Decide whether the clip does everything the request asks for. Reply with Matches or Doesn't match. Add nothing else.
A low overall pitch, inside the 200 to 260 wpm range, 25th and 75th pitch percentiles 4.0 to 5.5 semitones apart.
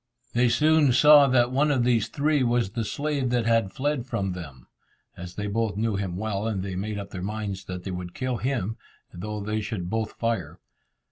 Matches